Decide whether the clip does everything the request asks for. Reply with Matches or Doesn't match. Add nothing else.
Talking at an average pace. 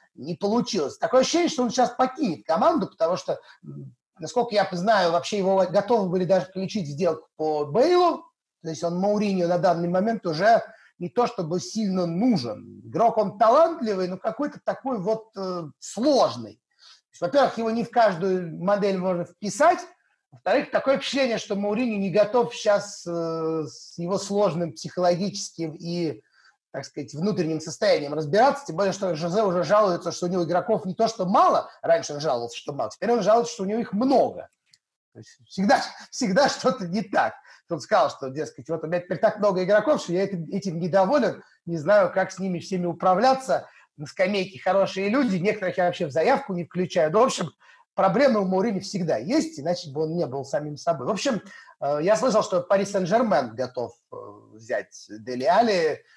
Doesn't match